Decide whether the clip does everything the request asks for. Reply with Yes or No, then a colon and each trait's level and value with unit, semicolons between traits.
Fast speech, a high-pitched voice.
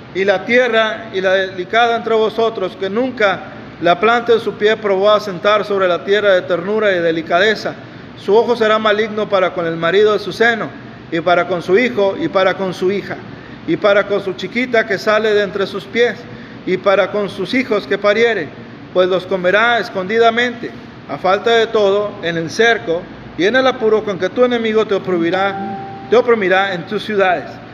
Yes: fast, 195 wpm; high, 200 Hz